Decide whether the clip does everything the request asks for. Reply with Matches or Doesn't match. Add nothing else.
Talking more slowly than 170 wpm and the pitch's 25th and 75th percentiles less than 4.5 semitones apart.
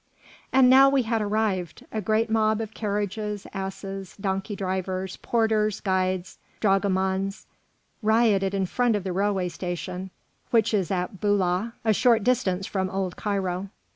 Matches